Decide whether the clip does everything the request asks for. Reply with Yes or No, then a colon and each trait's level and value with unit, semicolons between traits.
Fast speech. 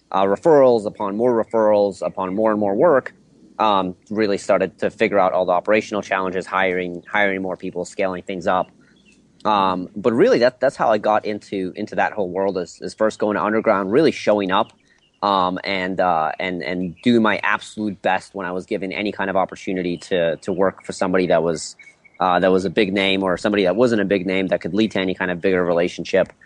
Yes: fast, 215 wpm